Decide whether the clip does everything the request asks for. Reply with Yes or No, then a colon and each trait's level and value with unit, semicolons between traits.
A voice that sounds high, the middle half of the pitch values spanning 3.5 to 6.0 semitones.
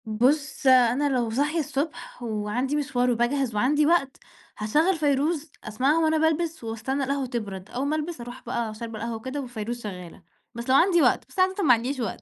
Yes: very high, 260 Hz; average, 4.3 semitones